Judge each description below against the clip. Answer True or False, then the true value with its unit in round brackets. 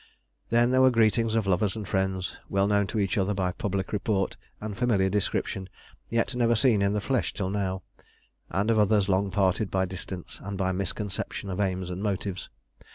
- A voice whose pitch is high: False (100 Hz)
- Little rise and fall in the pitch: True (2.3 semitones)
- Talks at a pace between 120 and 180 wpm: False (190 wpm)